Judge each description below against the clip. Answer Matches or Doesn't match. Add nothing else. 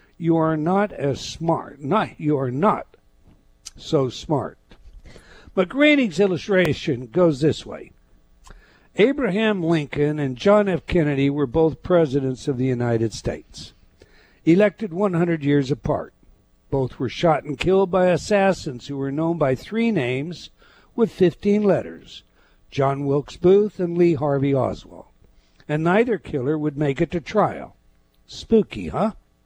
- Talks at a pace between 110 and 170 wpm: Matches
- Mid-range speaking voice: Matches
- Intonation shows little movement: Doesn't match